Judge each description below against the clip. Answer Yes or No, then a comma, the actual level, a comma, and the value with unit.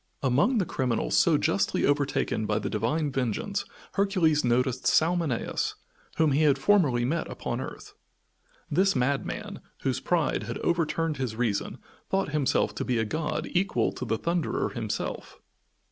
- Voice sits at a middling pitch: Yes, medium, 145 Hz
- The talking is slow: No, average, 145 wpm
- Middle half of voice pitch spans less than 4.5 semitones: No, average, 5.3 semitones